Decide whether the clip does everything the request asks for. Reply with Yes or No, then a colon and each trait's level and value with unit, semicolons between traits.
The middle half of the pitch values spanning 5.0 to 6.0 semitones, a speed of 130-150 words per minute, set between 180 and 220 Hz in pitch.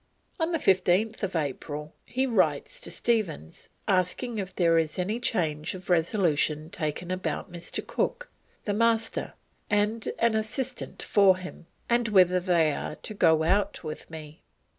Yes: average, 5.3 semitones; average, 140 wpm; medium, 185 Hz